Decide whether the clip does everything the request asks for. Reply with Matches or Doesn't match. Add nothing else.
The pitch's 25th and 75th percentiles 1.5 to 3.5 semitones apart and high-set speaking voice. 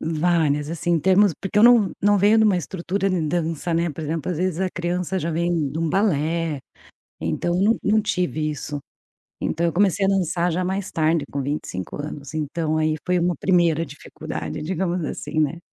Doesn't match